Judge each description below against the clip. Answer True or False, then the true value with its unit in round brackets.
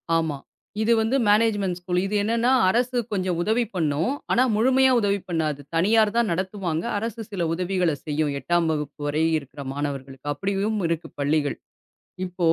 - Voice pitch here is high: False (180 Hz)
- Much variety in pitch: True (5.7 semitones)